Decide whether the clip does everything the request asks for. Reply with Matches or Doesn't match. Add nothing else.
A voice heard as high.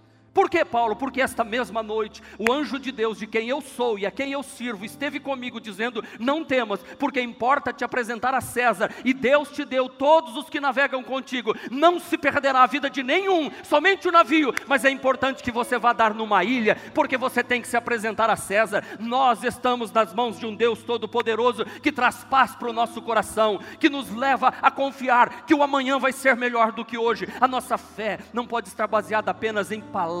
Matches